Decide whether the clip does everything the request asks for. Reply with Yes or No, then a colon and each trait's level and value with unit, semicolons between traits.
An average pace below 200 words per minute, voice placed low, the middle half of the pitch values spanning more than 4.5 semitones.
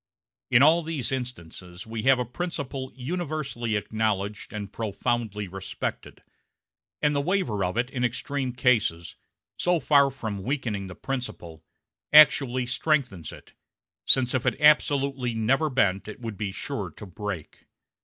Yes: average, 140 wpm; low, 125 Hz; average, 5.2 semitones